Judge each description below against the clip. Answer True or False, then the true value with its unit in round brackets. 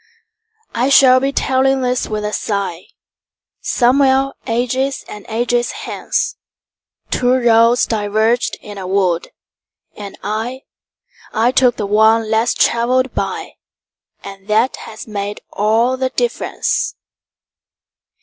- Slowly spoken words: True (100 wpm)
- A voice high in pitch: True (230 Hz)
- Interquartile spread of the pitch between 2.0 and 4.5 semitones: True (3.4 semitones)